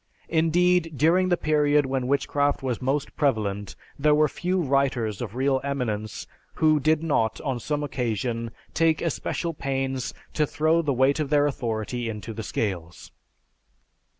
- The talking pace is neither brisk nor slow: Yes, average, 150 wpm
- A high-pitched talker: No, medium, 140 Hz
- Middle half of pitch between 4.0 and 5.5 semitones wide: Yes, average, 4.4 semitones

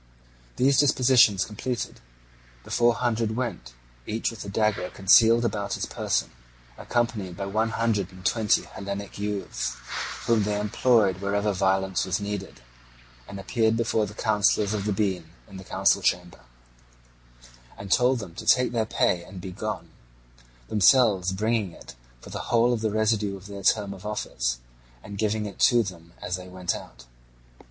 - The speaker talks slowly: No, average, 160 wpm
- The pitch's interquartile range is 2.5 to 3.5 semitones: Yes, average, 2.8 semitones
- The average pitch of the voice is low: Yes, low, 105 Hz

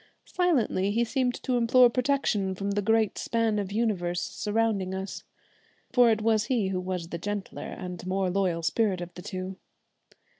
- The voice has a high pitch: Yes, high, 205 Hz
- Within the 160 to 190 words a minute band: Yes, average, 165 wpm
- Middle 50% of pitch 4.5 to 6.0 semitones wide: No, average, 3.6 semitones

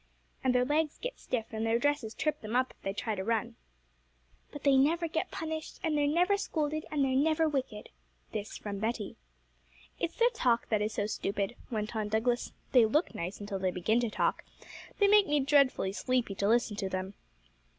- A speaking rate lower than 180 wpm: No, average, 200 wpm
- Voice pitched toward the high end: Yes, high, 245 Hz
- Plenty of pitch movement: Yes, wide, 6.0 semitones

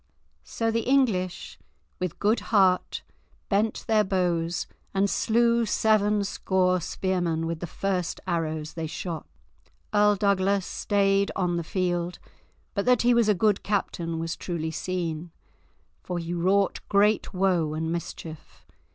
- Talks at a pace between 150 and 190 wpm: No, slow, 135 wpm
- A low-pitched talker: No, medium, 185 Hz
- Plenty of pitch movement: No, average, 3.3 semitones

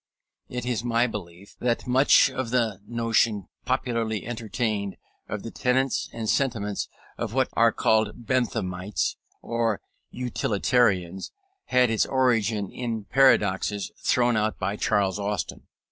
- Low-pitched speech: Yes, low, 115 Hz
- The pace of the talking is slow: Yes, slow, 125 wpm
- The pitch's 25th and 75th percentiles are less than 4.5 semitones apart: Yes, average, 3.2 semitones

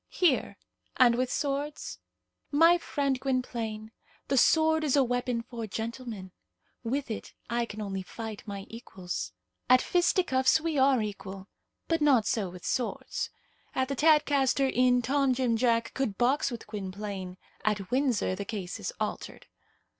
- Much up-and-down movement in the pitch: No, average, 4.3 semitones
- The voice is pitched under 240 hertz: No, high, 245 Hz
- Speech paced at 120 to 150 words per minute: Yes, average, 145 wpm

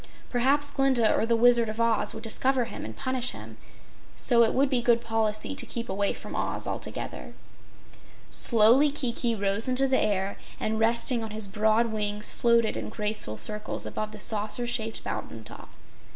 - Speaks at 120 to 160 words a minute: No, average, 175 wpm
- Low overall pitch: No, high, 230 Hz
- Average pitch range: No, narrow, 2.3 semitones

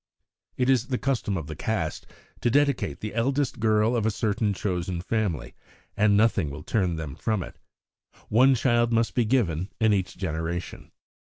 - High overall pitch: No, low, 105 Hz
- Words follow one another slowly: No, average, 170 wpm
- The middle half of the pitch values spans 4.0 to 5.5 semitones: Yes, average, 5.0 semitones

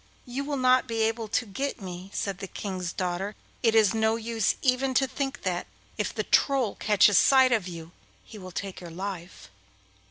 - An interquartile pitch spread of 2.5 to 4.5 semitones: No, average, 5.1 semitones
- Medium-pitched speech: No, high, 220 Hz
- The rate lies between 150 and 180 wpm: No, average, 195 wpm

